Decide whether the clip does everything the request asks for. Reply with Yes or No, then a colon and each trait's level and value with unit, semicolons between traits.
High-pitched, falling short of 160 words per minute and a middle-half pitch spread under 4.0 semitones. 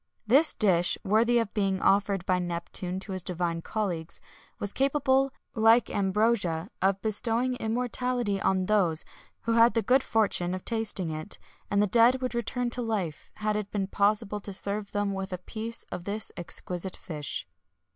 No: high, 205 Hz; average, 165 wpm; average, 3.6 semitones